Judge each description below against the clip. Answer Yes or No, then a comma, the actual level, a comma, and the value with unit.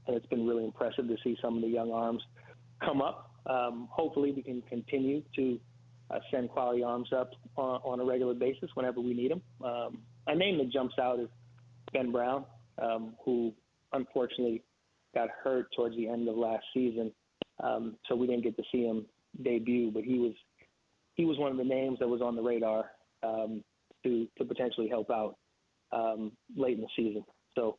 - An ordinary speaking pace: Yes, average, 190 wpm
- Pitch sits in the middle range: No, low, 120 Hz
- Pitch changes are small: Yes, narrow, 1.6 semitones